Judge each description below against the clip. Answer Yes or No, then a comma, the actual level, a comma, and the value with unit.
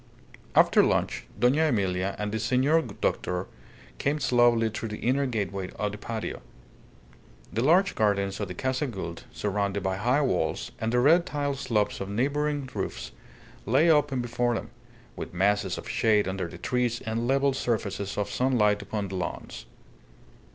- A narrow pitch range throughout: No, average, 4.7 semitones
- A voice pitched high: No, low, 115 Hz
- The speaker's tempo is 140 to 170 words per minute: Yes, average, 160 wpm